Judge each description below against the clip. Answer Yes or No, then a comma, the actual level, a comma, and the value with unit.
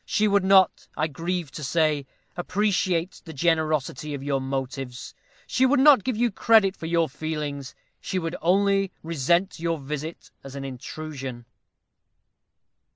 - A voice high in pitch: No, medium, 160 Hz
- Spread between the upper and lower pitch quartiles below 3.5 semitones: No, average, 5.2 semitones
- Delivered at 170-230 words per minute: No, average, 145 wpm